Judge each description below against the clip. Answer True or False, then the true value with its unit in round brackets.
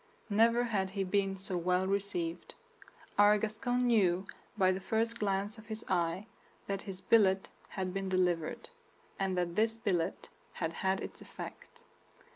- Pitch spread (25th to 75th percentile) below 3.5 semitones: True (2.6 semitones)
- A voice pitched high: True (195 Hz)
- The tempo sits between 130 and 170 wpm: True (150 wpm)